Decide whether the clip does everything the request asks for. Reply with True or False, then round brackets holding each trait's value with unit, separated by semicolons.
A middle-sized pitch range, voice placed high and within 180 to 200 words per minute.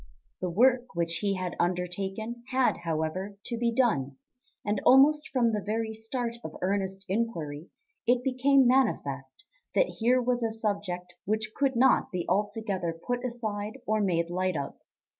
False (5.0 semitones; 215 Hz; 155 wpm)